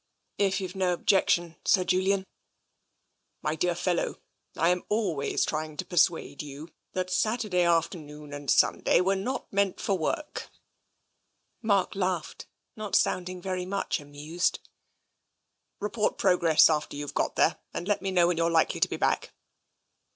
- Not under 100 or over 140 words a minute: No, average, 155 wpm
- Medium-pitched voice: Yes, medium, 180 Hz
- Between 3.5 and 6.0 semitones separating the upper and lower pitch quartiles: No, average, 3.1 semitones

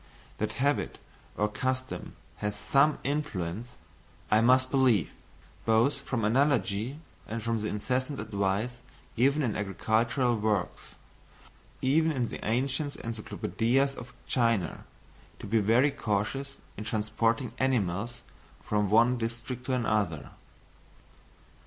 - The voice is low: Yes, low, 115 Hz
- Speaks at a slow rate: Yes, slow, 115 wpm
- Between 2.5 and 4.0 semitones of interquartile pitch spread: Yes, average, 3.5 semitones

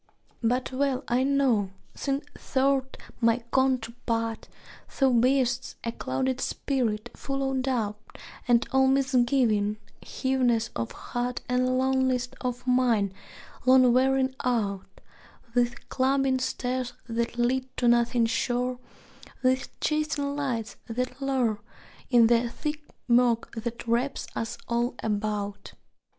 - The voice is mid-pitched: No, very high, 250 Hz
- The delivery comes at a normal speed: No, slow, 120 wpm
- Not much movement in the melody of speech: Yes, narrow, 2.1 semitones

